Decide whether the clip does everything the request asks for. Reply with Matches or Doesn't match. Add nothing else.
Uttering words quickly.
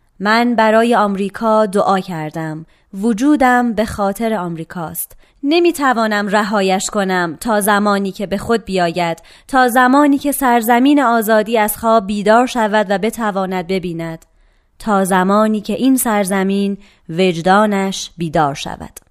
Doesn't match